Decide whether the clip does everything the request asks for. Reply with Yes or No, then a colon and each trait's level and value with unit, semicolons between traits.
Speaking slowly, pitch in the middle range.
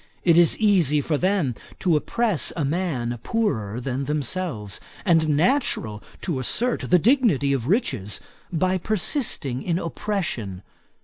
Yes: slow, 130 wpm; medium, 160 Hz